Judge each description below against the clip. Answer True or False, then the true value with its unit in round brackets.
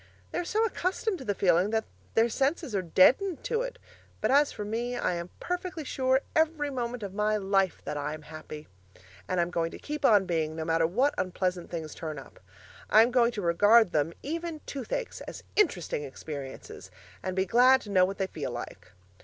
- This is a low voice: False (210 Hz)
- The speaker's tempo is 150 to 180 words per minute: False (200 wpm)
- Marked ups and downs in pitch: True (8.1 semitones)